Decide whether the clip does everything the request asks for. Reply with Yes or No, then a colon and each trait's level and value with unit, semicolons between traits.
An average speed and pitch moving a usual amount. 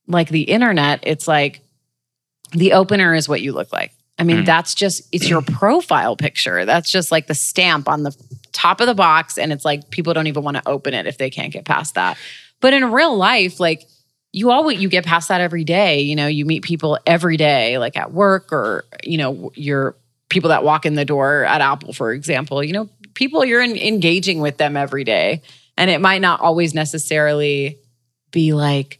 No: fast, 210 wpm; average, 3.9 semitones